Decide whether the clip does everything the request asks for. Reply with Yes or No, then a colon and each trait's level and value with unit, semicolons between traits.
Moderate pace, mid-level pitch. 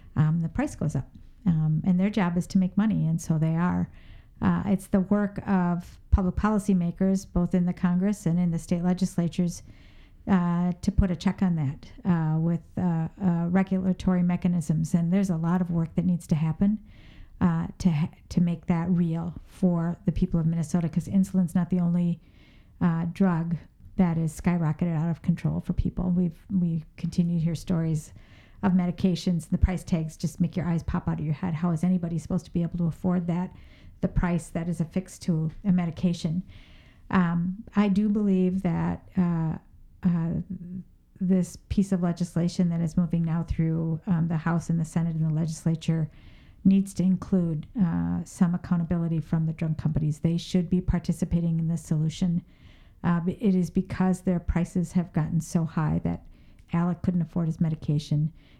Yes: average, 185 wpm; medium, 175 Hz